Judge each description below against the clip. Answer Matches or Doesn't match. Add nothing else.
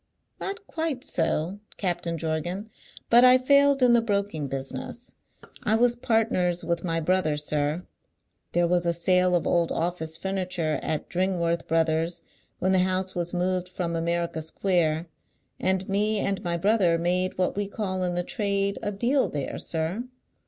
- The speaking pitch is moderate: Matches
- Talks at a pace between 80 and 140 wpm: Doesn't match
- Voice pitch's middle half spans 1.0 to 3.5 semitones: Matches